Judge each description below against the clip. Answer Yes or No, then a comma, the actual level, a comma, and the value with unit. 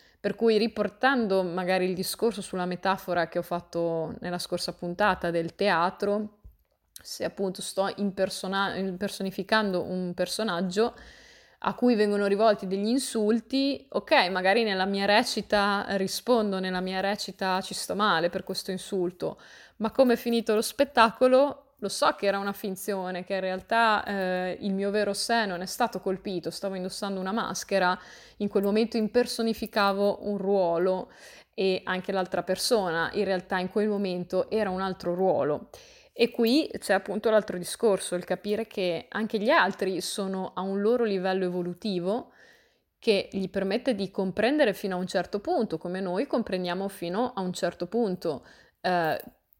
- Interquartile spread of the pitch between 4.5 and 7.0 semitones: No, average, 2.9 semitones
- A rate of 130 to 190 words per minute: Yes, average, 155 wpm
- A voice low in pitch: No, high, 195 Hz